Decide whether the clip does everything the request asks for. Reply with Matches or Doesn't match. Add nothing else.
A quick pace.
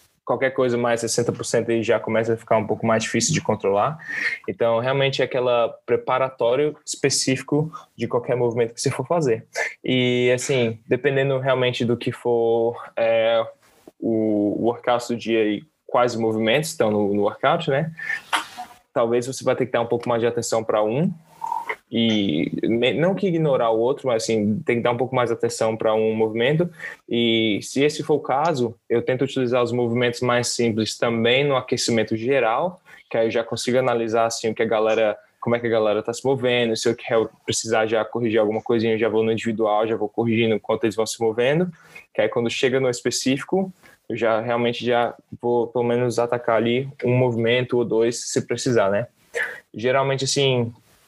Matches